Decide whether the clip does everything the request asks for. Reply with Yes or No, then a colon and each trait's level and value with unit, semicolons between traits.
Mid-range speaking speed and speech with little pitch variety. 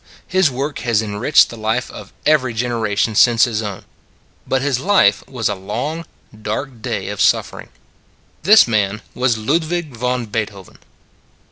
No: average, 145 wpm; average, 4.7 semitones